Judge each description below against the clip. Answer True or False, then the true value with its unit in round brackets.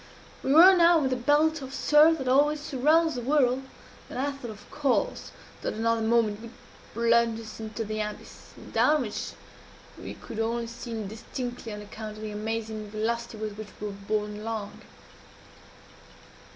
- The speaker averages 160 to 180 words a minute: True (165 wpm)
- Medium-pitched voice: False (230 Hz)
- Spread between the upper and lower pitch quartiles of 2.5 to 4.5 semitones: True (4.1 semitones)